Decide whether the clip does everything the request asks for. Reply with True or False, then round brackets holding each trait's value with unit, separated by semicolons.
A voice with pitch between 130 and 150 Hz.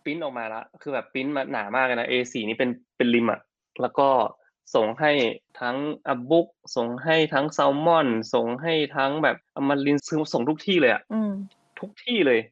True (140 Hz)